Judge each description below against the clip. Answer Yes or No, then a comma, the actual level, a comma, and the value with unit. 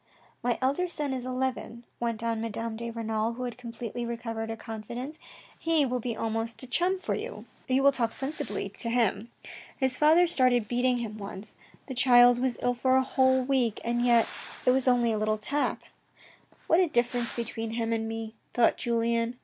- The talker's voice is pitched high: Yes, high, 240 Hz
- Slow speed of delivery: No, average, 190 wpm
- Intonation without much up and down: Yes, narrow, 2.2 semitones